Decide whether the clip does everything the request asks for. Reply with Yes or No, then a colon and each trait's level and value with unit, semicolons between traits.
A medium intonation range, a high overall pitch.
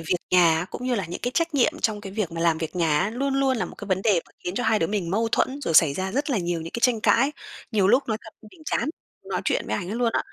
No: wide, 6.0 semitones; high, 205 Hz